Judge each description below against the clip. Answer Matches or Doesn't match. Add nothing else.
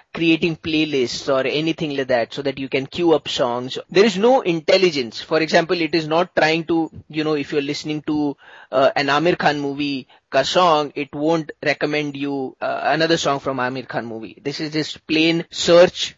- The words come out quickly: Doesn't match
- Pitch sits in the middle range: Matches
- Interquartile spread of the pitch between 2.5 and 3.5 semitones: Matches